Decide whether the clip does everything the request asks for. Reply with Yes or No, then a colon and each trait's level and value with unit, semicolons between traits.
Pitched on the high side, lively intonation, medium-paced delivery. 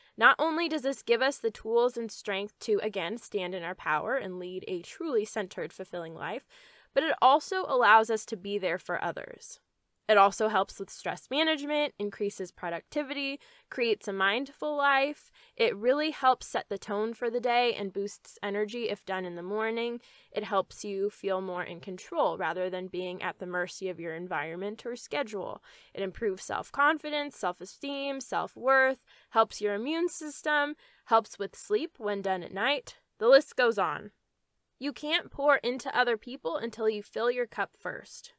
Yes: high, 225 Hz; wide, 6.3 semitones; average, 180 wpm